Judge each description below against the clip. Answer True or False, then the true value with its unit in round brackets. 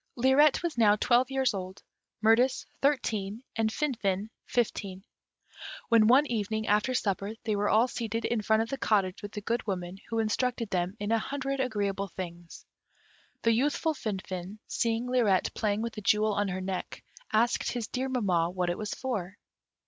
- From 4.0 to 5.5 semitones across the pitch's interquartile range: False (3.6 semitones)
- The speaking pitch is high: True (220 Hz)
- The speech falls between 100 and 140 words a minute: False (170 wpm)